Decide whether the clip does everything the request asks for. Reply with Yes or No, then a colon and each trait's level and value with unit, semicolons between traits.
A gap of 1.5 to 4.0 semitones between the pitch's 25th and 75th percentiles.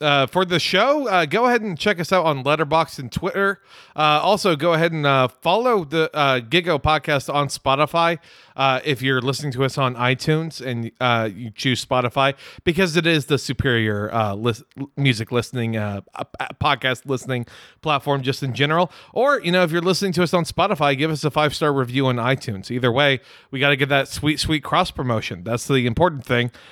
No: average, 4.4 semitones